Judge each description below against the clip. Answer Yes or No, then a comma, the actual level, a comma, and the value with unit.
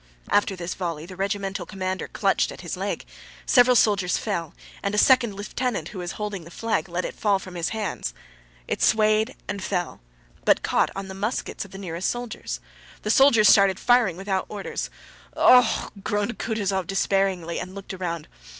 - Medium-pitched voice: No, high, 195 Hz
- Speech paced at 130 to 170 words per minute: No, average, 180 wpm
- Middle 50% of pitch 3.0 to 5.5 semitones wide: No, narrow, 2.6 semitones